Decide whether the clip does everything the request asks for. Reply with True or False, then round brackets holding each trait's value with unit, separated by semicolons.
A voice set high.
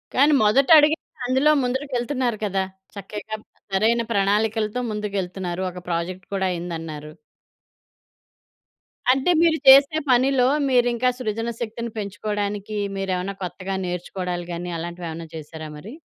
True (205 Hz)